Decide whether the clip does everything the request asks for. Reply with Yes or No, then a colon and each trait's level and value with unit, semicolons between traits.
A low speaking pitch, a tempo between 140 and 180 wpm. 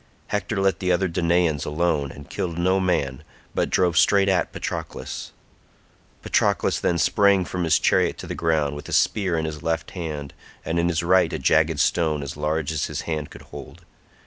No: very low, 85 Hz; average, 190 wpm